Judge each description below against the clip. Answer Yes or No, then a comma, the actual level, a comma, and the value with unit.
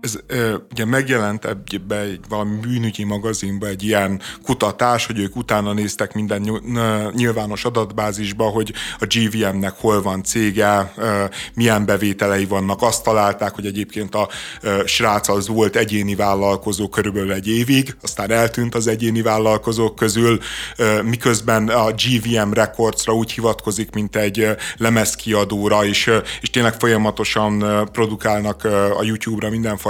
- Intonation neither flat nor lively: No, narrow, 1.6 semitones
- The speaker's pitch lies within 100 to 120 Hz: Yes, low, 110 Hz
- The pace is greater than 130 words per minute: No, average, 125 wpm